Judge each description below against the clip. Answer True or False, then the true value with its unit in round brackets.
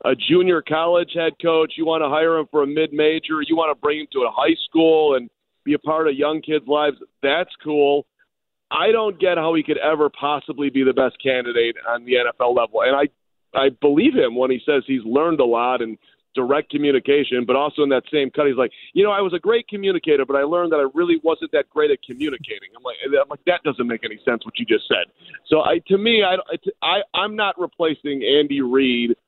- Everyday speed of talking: False (235 wpm)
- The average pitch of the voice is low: False (155 Hz)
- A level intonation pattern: False (4.0 semitones)